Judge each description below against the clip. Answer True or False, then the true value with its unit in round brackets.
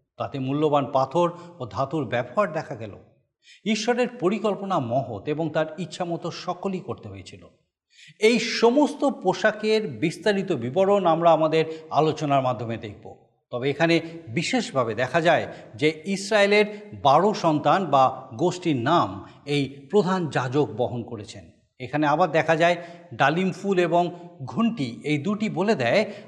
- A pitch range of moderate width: False (6.3 semitones)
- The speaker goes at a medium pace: False (130 wpm)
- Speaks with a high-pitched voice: False (165 Hz)